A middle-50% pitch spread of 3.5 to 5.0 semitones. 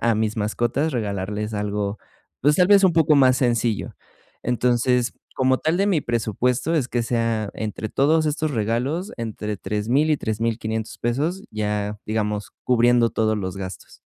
Yes: average, 4.2 semitones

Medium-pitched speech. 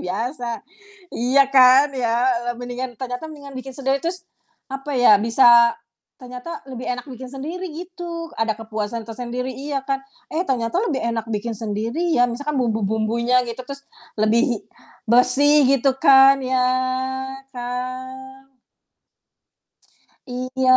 No: very high, 255 Hz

